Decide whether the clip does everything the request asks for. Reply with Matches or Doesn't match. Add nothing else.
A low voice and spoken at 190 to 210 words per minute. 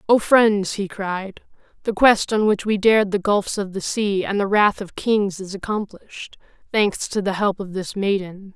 Doesn't match